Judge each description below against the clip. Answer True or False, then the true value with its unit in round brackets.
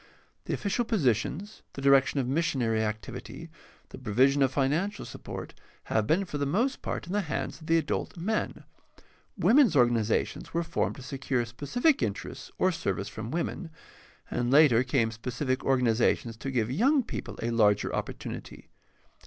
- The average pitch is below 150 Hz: True (135 Hz)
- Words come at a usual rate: True (155 wpm)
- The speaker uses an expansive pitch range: True (6.3 semitones)